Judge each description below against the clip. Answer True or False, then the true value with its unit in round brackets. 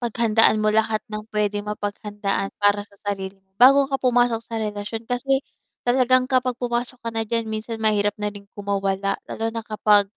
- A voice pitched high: True (215 Hz)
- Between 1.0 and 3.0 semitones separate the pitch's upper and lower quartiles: True (2.6 semitones)